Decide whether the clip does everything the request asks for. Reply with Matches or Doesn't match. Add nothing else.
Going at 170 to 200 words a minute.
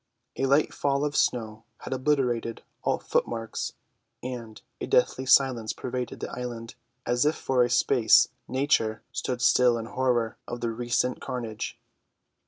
Doesn't match